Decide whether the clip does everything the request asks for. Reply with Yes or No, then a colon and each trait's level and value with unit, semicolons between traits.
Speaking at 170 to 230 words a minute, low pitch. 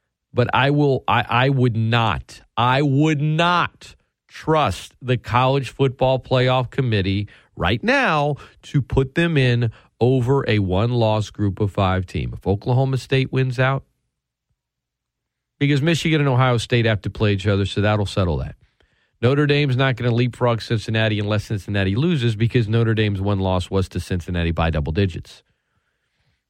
No: average, 160 wpm; low, 120 Hz